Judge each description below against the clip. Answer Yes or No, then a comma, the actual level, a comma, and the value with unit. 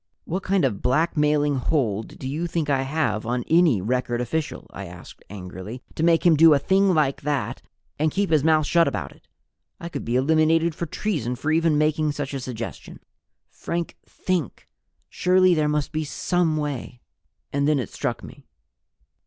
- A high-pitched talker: No, medium, 150 Hz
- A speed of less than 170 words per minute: No, average, 180 wpm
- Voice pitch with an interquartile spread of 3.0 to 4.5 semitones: Yes, average, 4.0 semitones